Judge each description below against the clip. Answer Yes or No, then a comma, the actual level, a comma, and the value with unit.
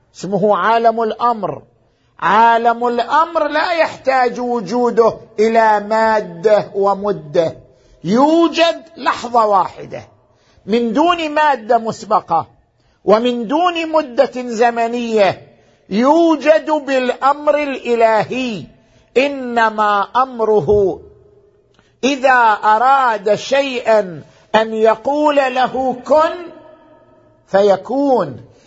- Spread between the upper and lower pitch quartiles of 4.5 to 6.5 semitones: Yes, average, 5.1 semitones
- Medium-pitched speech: No, high, 235 Hz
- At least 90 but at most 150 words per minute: No, average, 75 wpm